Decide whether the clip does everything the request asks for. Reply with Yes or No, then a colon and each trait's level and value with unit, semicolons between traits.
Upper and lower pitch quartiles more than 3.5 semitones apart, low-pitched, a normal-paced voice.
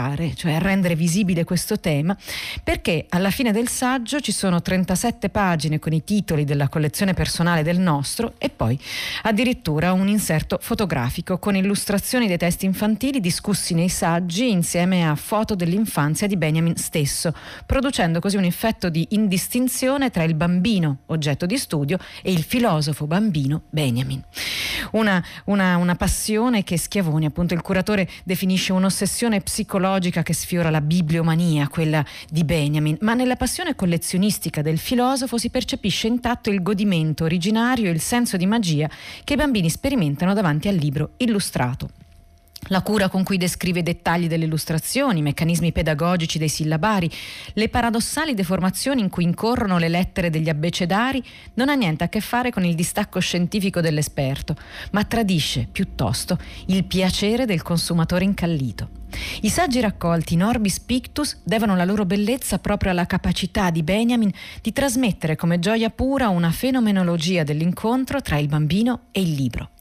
No: average, 4.7 semitones; medium, 185 Hz; average, 150 wpm